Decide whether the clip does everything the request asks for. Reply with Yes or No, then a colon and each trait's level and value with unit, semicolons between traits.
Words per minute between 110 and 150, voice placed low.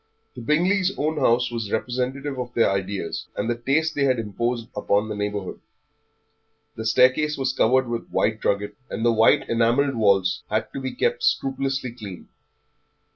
No: average, 165 wpm; low, 120 Hz